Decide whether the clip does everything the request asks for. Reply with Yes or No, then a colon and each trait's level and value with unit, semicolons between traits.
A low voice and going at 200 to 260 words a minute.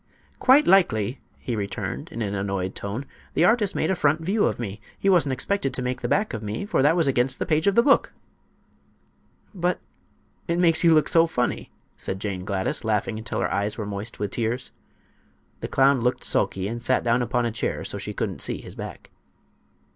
Yes: low, 125 Hz; fast, 205 wpm